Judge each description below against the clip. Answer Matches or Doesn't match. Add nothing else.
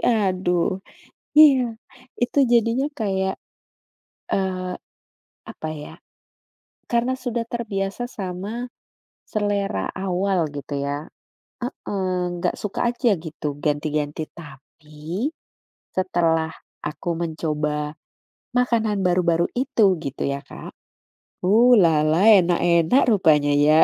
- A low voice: Doesn't match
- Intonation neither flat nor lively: Doesn't match